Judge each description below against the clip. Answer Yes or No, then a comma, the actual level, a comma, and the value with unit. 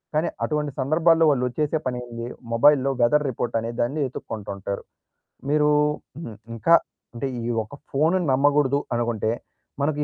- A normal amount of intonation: Yes, average, 4.1 semitones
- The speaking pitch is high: No, low, 135 Hz